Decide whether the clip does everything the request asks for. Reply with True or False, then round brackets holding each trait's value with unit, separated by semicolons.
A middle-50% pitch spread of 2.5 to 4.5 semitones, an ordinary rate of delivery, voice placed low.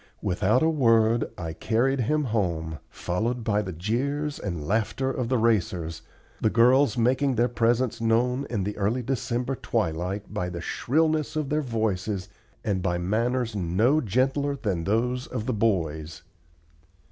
False (5.0 semitones; 150 wpm; 115 Hz)